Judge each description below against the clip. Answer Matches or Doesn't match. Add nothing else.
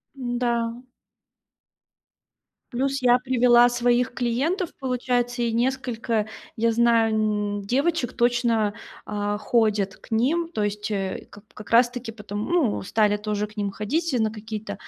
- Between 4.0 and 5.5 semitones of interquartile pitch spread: Doesn't match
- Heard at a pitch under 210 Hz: Doesn't match